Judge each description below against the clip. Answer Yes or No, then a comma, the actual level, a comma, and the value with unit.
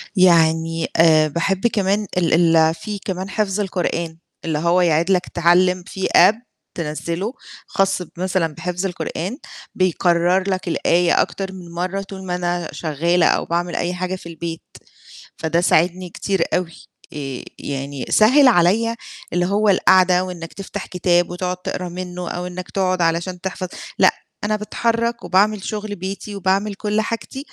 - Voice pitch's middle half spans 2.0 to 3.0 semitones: Yes, narrow, 2.4 semitones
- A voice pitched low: No, medium, 180 Hz